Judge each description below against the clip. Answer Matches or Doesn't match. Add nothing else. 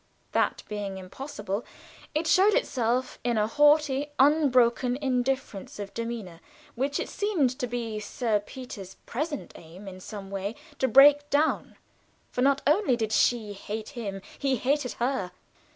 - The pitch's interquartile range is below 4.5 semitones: Doesn't match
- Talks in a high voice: Matches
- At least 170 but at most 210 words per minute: Doesn't match